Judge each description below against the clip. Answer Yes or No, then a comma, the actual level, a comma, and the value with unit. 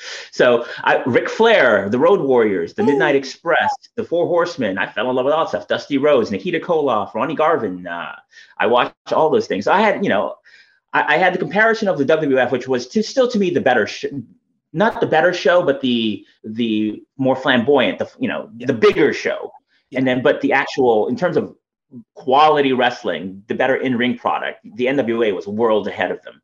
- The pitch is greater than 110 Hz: Yes, medium, 140 Hz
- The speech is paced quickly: Yes, fast, 210 wpm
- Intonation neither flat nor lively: No, wide, 7.5 semitones